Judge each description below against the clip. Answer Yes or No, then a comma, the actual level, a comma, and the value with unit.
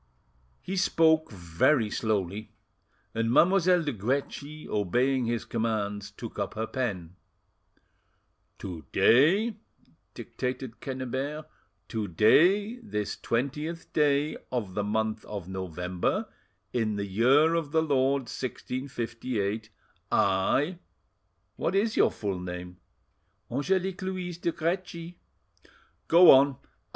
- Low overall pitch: Yes, low, 125 Hz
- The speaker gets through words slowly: Yes, slow, 105 wpm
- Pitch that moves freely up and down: Yes, wide, 7.3 semitones